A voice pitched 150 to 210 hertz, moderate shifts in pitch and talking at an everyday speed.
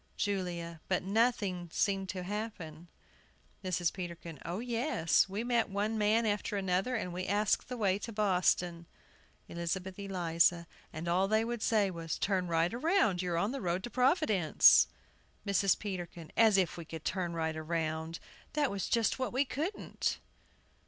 Yes: high, 190 Hz; average, 4.2 semitones; average, 160 wpm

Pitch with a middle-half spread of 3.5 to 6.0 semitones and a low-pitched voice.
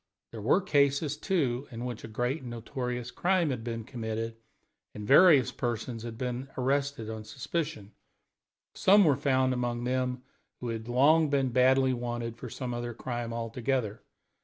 No: average, 2.8 semitones; low, 125 Hz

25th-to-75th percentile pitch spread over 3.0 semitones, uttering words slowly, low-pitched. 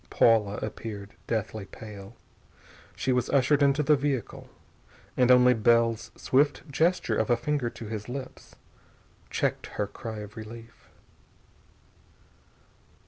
Yes: average, 3.6 semitones; slow, 120 wpm; low, 115 Hz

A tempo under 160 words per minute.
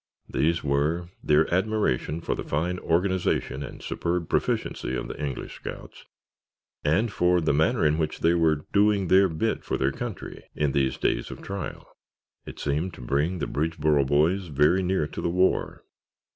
No: average, 170 wpm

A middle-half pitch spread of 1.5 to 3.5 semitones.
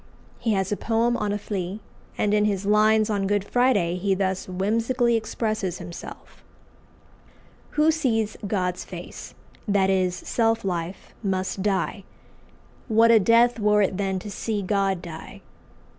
Yes: average, 2.9 semitones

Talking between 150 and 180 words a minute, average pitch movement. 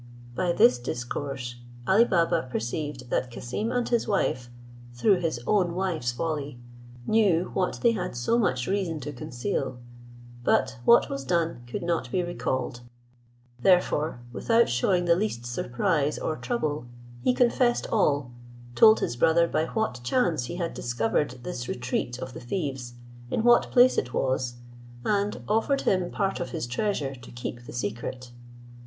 No: average, 155 wpm; wide, 7.7 semitones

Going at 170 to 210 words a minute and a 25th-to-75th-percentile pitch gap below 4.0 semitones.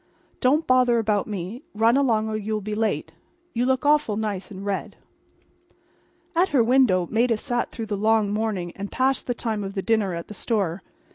Yes: average, 190 wpm; average, 3.2 semitones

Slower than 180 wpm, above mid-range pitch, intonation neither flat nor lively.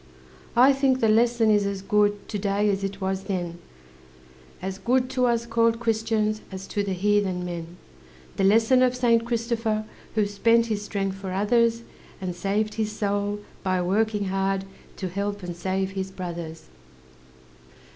Yes: average, 160 wpm; high, 205 Hz; average, 3.0 semitones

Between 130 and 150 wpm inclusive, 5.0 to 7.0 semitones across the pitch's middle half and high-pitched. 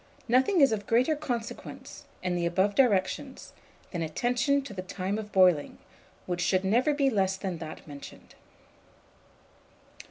Yes: average, 140 wpm; wide, 5.5 semitones; high, 200 Hz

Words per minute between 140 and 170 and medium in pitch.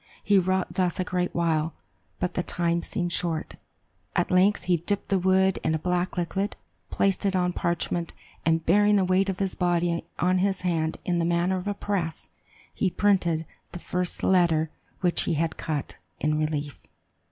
No: average, 180 wpm; medium, 180 Hz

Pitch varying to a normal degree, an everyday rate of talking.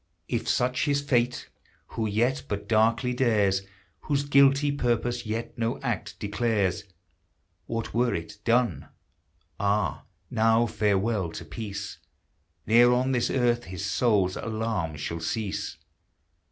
No: average, 3.4 semitones; slow, 125 wpm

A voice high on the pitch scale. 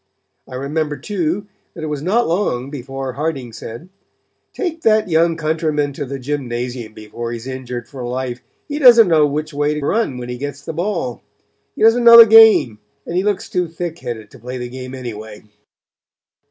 No: medium, 145 Hz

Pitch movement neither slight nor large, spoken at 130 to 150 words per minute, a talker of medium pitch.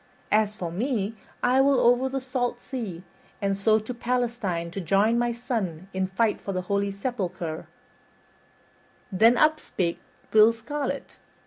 No: average, 4.2 semitones; average, 145 wpm; high, 220 Hz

